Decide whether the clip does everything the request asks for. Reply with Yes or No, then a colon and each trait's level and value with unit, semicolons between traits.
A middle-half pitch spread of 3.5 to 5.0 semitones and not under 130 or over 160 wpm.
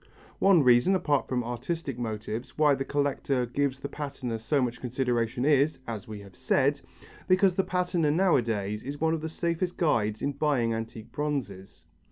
No: average, 4.6 semitones; average, 170 wpm